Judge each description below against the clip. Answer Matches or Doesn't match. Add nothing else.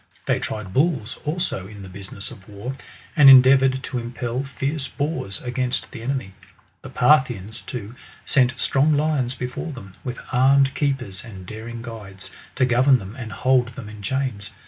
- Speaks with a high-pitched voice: Doesn't match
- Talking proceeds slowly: Doesn't match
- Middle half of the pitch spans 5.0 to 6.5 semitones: Doesn't match